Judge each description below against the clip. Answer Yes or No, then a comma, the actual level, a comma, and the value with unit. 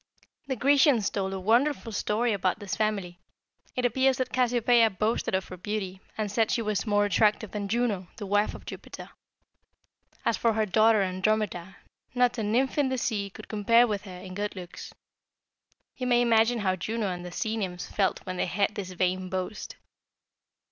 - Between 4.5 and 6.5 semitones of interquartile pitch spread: No, average, 3.5 semitones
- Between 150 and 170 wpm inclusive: No, average, 185 wpm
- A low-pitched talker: No, high, 210 Hz